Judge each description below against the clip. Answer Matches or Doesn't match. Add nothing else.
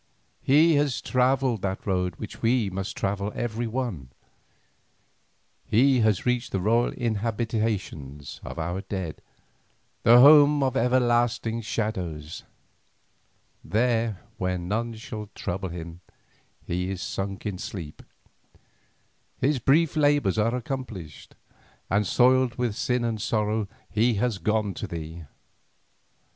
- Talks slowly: Matches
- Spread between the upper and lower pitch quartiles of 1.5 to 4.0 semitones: Doesn't match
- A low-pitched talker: Matches